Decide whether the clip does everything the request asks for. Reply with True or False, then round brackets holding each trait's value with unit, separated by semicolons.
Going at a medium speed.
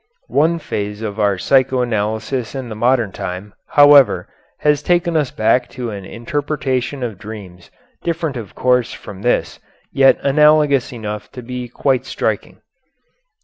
True (145 wpm)